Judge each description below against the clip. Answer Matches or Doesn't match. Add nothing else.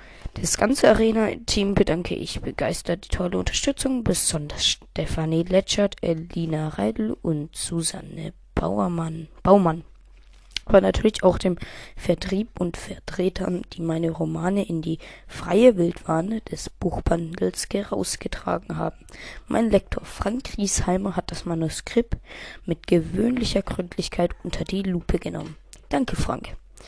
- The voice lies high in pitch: Doesn't match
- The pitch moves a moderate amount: Matches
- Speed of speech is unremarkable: Doesn't match